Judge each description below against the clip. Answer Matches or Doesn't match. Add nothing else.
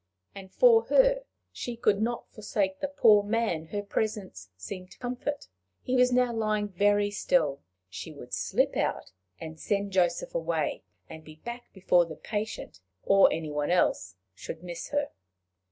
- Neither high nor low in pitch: Doesn't match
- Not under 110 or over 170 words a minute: Matches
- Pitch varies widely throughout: Matches